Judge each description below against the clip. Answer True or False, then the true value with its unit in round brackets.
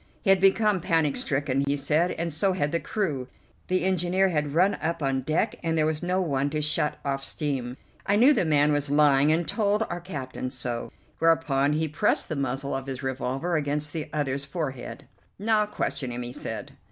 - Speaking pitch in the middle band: True (150 Hz)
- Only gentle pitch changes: False (4.2 semitones)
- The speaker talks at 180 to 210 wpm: True (200 wpm)